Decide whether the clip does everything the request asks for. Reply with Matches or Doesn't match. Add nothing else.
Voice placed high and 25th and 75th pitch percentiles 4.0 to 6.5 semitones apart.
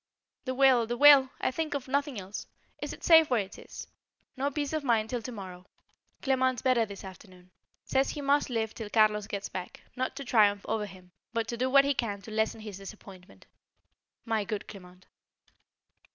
Matches